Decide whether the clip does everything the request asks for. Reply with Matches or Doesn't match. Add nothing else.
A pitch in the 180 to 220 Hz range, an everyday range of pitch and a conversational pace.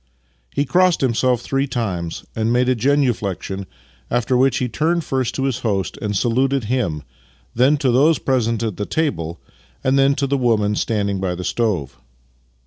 Doesn't match